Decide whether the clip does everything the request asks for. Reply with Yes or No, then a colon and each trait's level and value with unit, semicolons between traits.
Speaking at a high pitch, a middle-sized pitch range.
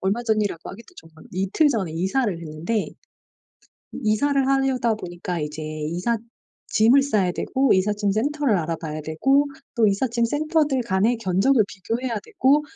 No: high, 220 Hz; wide, 6.5 semitones